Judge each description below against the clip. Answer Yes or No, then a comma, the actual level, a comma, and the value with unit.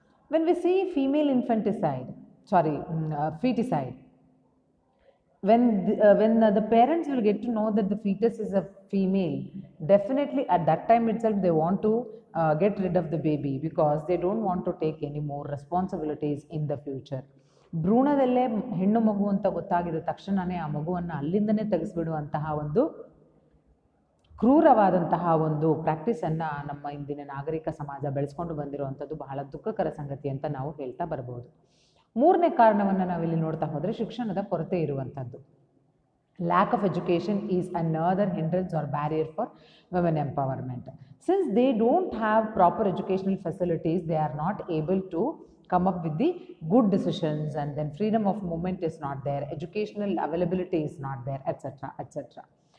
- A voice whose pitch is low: No, medium, 175 Hz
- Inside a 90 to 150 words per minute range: Yes, average, 145 wpm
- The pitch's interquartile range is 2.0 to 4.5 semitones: No, wide, 5.5 semitones